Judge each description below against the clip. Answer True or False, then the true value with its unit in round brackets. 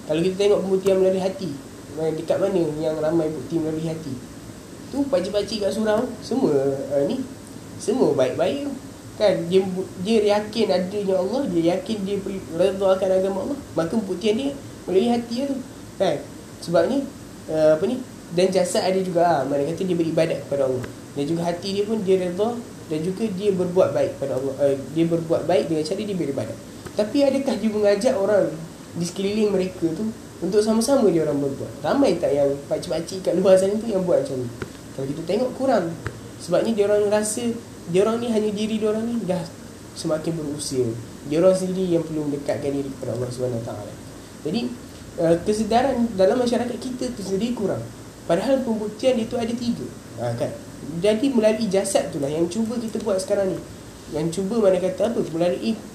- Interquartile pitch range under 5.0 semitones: False (5.4 semitones)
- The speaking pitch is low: False (190 Hz)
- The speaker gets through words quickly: True (180 wpm)